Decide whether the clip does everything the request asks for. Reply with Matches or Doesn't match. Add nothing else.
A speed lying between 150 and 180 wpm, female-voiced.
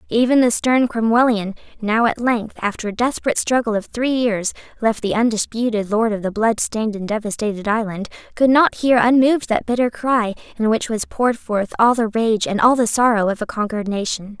Doesn't match